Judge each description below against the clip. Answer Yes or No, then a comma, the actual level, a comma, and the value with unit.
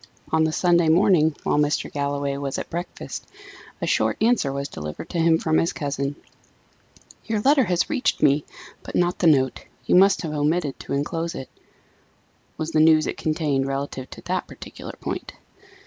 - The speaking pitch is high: No, medium, 155 Hz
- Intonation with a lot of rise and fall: No, average, 3.5 semitones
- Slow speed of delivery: No, average, 175 wpm